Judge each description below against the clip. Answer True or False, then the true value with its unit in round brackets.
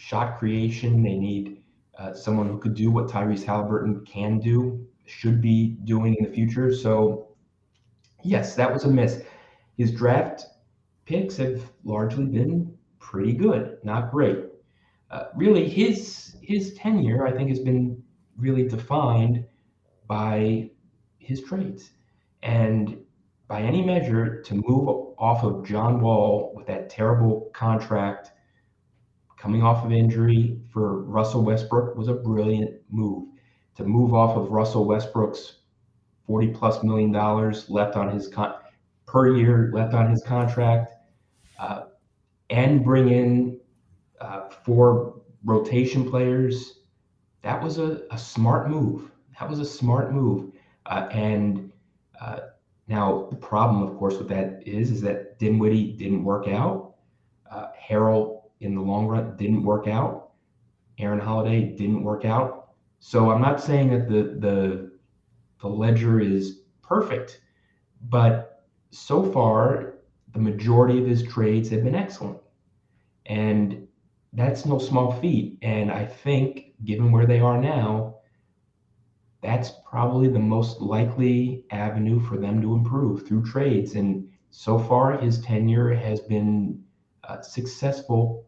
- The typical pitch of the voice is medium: False (115 Hz)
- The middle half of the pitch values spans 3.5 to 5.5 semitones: False (2.6 semitones)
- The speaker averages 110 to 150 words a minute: True (135 wpm)